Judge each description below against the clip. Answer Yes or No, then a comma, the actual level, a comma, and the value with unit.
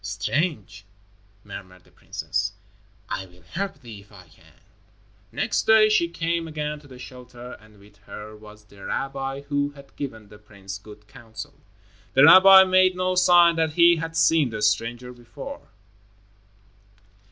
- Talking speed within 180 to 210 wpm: No, average, 150 wpm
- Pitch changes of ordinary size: No, wide, 7.8 semitones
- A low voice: Yes, low, 125 Hz